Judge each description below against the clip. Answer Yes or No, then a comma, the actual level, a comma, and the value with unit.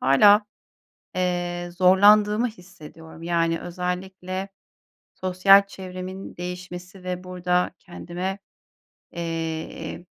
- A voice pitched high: No, medium, 180 Hz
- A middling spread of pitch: No, narrow, 1.4 semitones